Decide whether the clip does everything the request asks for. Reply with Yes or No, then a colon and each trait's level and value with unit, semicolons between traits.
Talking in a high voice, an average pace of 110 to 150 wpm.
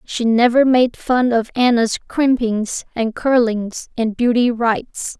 Yes: high, 235 Hz; average, 140 wpm